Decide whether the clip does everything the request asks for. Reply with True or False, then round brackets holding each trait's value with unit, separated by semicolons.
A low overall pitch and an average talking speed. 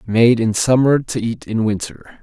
True (115 Hz; 190 wpm)